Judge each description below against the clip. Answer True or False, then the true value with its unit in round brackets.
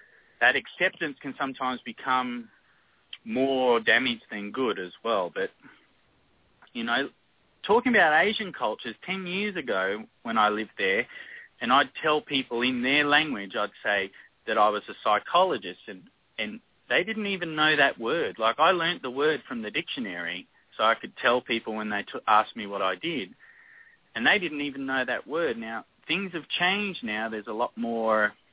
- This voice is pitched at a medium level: True (145 Hz)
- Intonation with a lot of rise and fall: True (8.7 semitones)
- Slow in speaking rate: False (175 wpm)